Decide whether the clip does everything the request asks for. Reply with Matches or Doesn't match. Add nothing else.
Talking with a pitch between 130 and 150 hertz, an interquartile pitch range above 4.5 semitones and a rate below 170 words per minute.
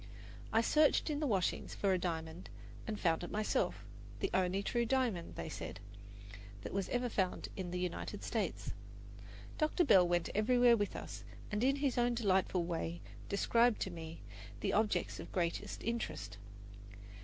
Doesn't match